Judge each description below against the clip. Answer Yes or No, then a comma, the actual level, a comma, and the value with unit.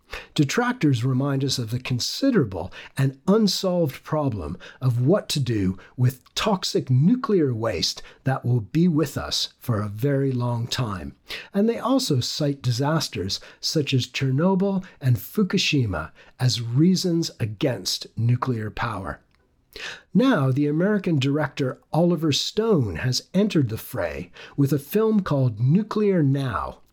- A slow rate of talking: Yes, slow, 130 wpm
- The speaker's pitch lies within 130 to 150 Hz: Yes, medium, 140 Hz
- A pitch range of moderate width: No, wide, 6.0 semitones